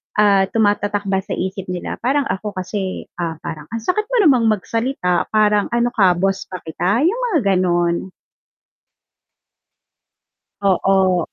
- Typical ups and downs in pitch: Yes, average, 3.6 semitones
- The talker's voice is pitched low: No, high, 195 Hz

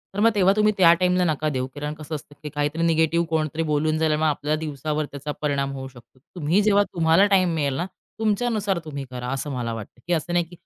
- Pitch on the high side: No, medium, 155 Hz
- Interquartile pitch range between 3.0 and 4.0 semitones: Yes, average, 3.3 semitones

